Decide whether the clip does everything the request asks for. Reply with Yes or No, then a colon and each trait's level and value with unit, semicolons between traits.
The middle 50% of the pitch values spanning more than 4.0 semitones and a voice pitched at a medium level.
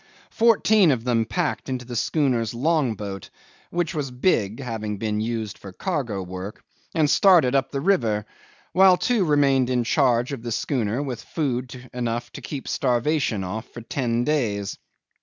No: average, 4.7 semitones; low, 125 Hz